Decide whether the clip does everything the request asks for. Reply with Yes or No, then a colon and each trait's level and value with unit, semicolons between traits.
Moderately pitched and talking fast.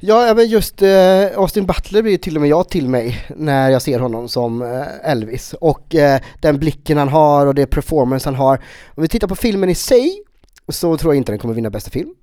Yes: medium, 155 Hz; fast, 215 wpm